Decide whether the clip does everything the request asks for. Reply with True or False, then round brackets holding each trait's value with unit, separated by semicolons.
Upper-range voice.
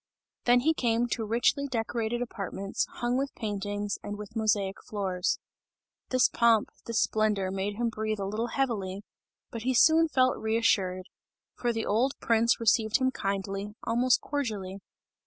True (225 Hz)